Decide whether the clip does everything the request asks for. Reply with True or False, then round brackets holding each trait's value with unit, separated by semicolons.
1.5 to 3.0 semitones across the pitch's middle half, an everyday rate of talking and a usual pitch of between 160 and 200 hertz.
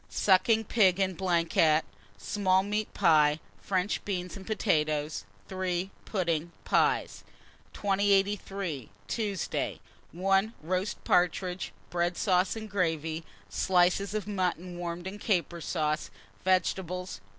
False (2.6 semitones; 105 wpm; 185 Hz)